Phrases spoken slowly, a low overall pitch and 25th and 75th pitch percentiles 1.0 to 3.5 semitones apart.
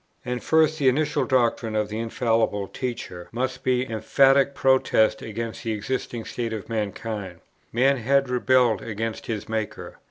No: average, 155 wpm; low, 115 Hz; average, 3.0 semitones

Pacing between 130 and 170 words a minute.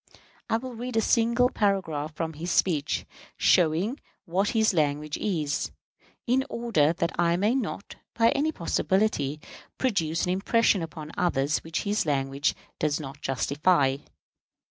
Yes: average, 140 wpm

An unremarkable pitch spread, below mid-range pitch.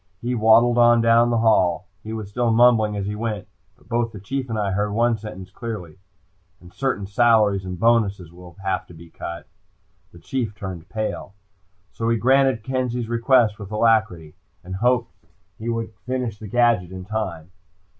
Yes: average, 3.5 semitones; low, 110 Hz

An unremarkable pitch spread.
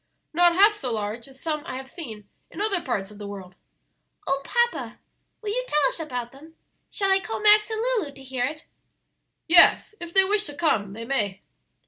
No: wide, 8.3 semitones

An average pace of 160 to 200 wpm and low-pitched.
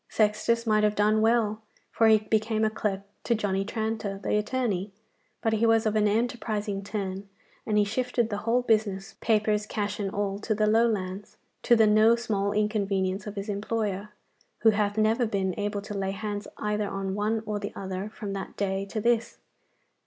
No: average, 180 wpm; high, 210 Hz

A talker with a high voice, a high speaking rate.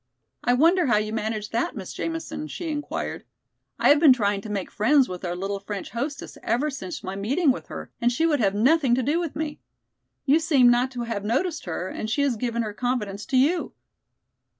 Yes: high, 245 Hz; fast, 215 wpm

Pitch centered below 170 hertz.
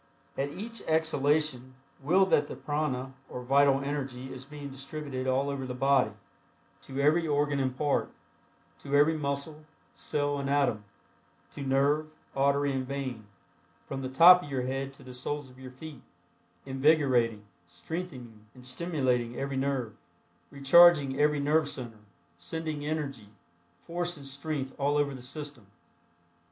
Yes: medium, 140 Hz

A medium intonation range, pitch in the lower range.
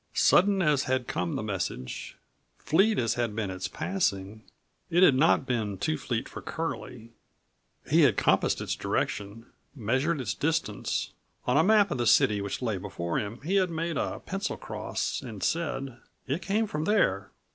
No: wide, 7.6 semitones; low, 130 Hz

